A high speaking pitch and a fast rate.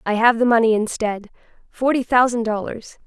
No: high, 230 Hz; slow, 135 wpm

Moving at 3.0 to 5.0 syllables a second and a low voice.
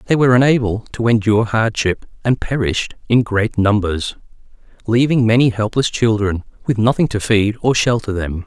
No: 5.3 syllables/s; low, 110 Hz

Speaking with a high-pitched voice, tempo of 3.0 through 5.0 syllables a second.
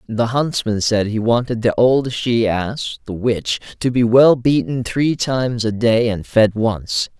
No: low, 115 Hz; 4.0 syllables/s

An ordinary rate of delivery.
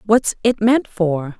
Yes: average, 170 wpm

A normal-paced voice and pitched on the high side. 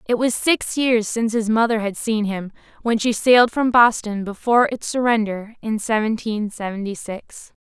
Yes: average, 175 wpm; high, 220 Hz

